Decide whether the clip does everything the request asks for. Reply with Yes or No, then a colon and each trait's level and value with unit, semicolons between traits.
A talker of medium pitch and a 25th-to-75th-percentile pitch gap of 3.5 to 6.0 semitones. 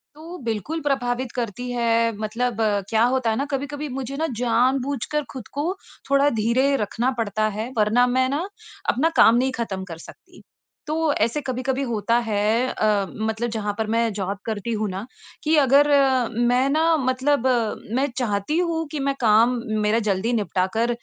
No: high, 240 Hz; average, 4.0 semitones